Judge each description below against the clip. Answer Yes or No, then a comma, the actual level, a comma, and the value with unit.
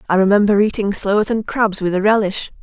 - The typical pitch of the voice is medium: No, high, 205 Hz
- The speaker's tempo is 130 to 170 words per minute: No, fast, 205 wpm